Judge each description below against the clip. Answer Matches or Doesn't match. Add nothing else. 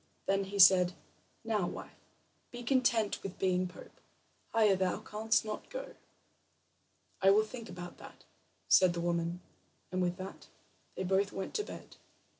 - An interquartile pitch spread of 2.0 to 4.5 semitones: Matches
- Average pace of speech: Matches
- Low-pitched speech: Doesn't match